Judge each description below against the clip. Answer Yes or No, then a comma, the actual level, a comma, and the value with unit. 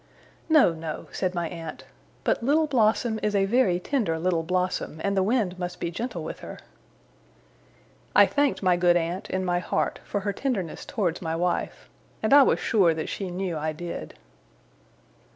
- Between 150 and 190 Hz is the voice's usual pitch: Yes, medium, 185 Hz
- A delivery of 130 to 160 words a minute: No, average, 175 wpm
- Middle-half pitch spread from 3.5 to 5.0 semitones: Yes, average, 3.9 semitones